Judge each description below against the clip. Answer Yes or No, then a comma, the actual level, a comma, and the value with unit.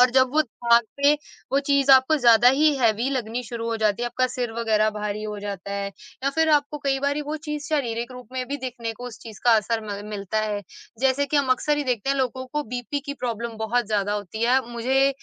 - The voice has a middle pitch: No, high, 245 Hz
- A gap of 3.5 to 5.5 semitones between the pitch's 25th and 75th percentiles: Yes, average, 3.8 semitones